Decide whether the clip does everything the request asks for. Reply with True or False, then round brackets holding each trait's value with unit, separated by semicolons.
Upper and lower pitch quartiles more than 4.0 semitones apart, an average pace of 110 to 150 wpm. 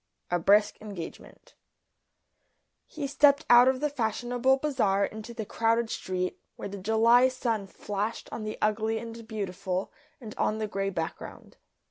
False (3.3 semitones; 145 wpm)